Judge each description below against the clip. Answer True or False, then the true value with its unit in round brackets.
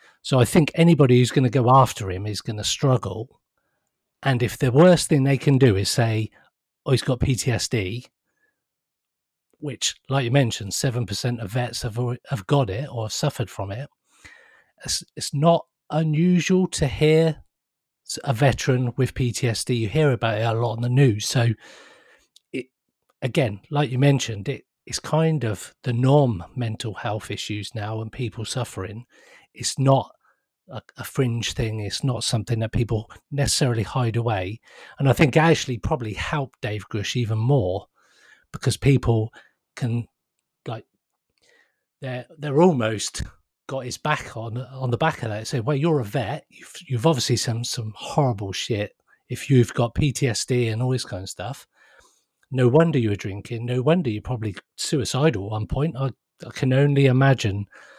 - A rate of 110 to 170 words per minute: True (165 wpm)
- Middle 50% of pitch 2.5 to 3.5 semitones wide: False (3.9 semitones)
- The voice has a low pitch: True (125 Hz)